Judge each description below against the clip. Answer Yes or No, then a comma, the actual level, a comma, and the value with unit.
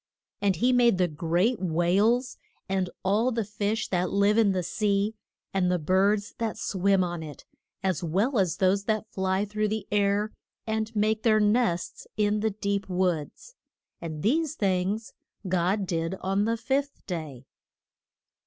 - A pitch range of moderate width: Yes, average, 3.1 semitones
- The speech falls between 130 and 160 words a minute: Yes, average, 155 wpm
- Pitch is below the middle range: No, high, 200 Hz